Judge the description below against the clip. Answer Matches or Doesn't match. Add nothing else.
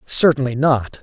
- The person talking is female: Doesn't match